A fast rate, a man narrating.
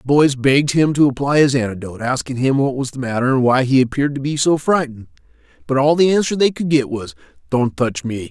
Yes: fast, 240 wpm; male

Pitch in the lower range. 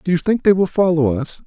No: medium, 170 Hz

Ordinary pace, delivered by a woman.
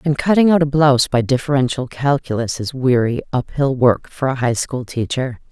Yes: average, 175 wpm; female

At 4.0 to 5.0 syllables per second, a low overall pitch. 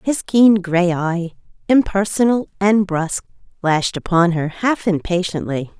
No: 4.3 syllables/s; medium, 185 Hz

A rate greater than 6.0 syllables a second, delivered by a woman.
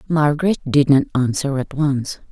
No: 4.9 syllables/s; female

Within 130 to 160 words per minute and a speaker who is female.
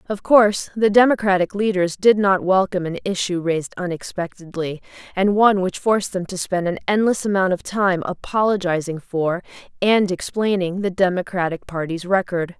Yes: average, 150 wpm; female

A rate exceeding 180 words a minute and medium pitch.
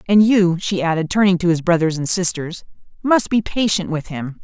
Yes: fast, 205 wpm; medium, 180 Hz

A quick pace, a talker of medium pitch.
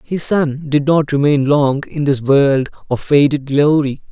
No: average, 175 wpm; medium, 145 Hz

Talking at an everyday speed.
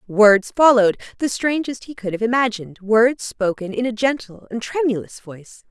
Yes: average, 170 wpm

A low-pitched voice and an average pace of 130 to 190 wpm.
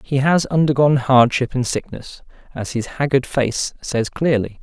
Yes: low, 130 Hz; average, 155 wpm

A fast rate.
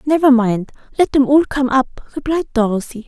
No: average, 175 wpm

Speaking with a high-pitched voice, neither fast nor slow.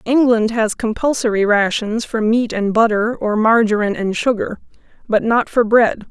Yes: high, 220 Hz; average, 155 wpm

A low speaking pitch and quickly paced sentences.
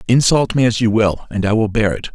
Yes: low, 110 Hz; fast, 280 wpm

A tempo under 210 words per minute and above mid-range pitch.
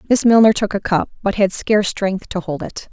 No: fast, 245 wpm; high, 205 Hz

